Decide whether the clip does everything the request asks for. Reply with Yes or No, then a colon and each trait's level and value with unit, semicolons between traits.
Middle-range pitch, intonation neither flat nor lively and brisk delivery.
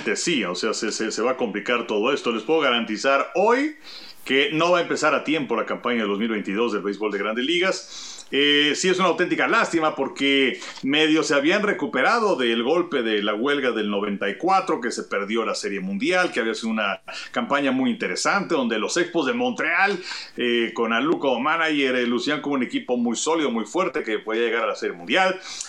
No: medium, 145 Hz; wide, 7.4 semitones; fast, 205 wpm